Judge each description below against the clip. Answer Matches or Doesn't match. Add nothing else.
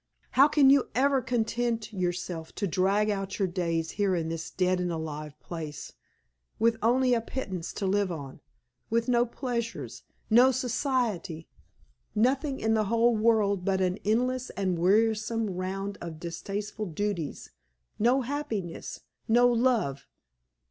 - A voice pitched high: Matches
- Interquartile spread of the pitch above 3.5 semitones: Matches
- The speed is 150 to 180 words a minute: Doesn't match